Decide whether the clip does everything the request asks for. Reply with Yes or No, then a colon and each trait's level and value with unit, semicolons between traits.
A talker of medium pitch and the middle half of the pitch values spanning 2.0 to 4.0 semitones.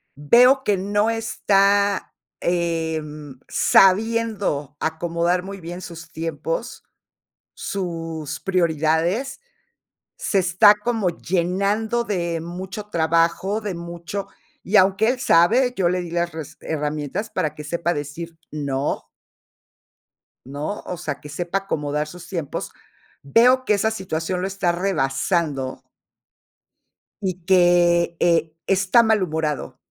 Yes: medium, 175 Hz; average, 3.7 semitones